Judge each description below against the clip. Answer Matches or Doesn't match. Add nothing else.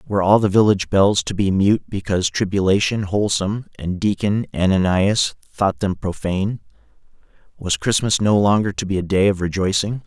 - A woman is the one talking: Doesn't match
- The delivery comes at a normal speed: Matches